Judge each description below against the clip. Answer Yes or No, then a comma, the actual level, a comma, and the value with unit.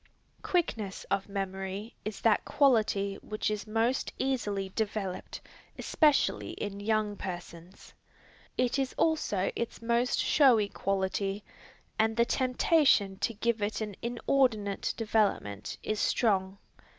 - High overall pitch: Yes, high, 215 Hz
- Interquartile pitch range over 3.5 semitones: No, average, 3.1 semitones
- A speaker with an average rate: No, slow, 115 wpm